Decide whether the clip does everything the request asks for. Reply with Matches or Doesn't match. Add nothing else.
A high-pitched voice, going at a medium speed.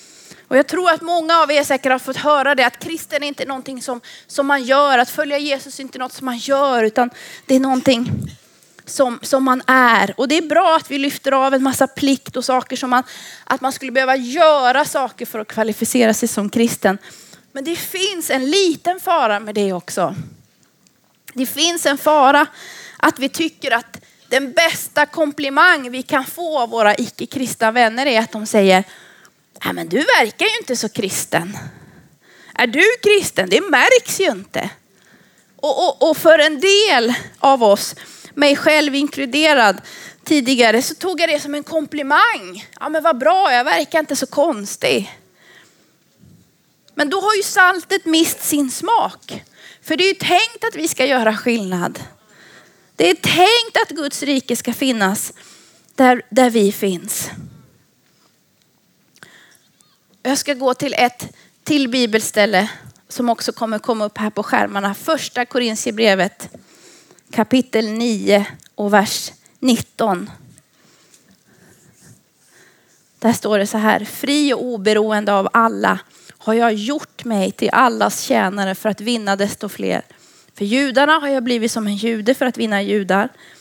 Matches